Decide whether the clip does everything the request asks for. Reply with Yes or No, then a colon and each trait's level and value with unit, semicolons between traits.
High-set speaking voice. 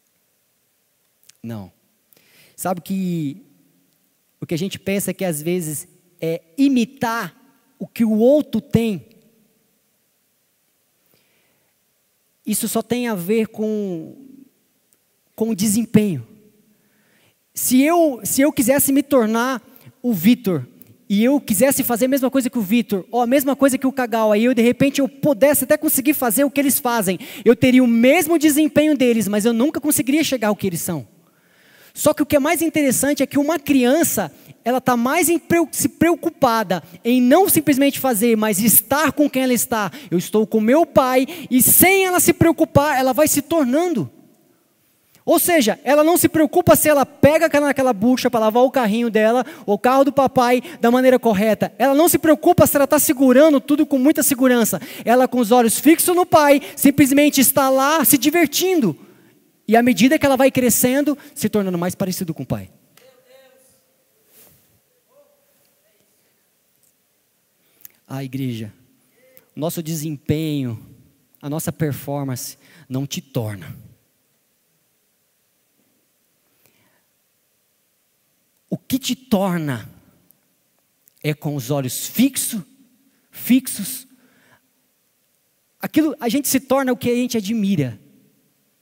Yes: very high, 250 Hz